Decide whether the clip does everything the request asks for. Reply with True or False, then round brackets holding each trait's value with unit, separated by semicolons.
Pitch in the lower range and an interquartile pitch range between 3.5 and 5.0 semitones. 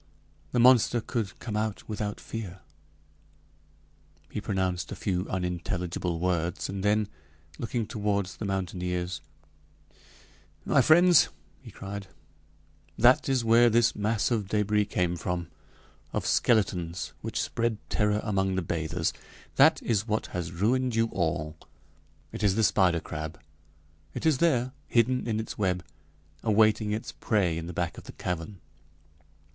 True (100 Hz; 4.0 semitones)